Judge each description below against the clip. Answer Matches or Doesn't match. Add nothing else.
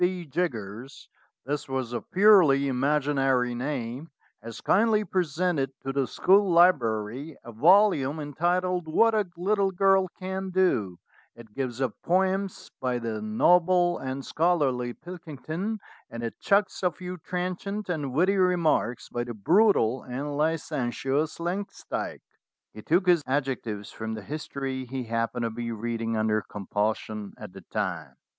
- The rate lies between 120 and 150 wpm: Matches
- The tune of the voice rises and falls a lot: Matches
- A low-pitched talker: Doesn't match